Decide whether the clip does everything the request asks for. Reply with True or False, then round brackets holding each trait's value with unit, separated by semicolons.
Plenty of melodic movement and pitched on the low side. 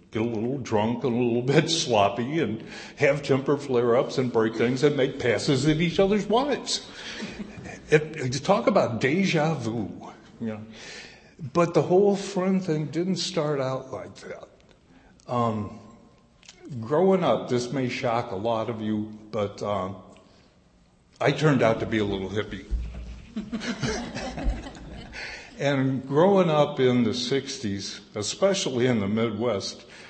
True (6.2 semitones; 130 Hz)